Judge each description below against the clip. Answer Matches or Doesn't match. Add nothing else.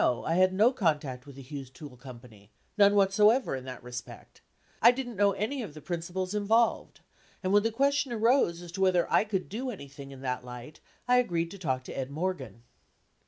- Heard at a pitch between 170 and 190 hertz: Matches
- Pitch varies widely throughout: Matches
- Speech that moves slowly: Doesn't match